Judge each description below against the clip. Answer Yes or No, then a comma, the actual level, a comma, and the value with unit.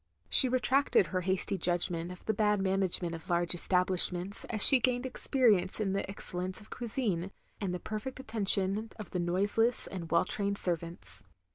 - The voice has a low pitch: No, high, 195 Hz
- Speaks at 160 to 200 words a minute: Yes, average, 165 wpm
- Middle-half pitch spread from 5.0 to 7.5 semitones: No, average, 3.4 semitones